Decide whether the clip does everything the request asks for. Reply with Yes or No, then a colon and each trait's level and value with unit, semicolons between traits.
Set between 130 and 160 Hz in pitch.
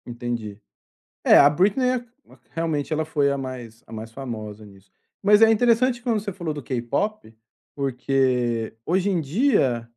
Yes: medium, 140 Hz